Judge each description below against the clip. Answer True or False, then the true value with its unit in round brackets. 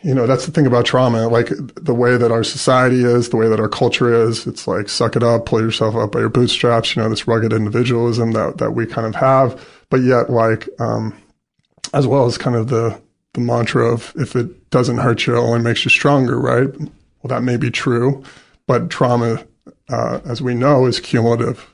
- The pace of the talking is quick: True (220 wpm)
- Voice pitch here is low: True (120 Hz)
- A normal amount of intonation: False (1.8 semitones)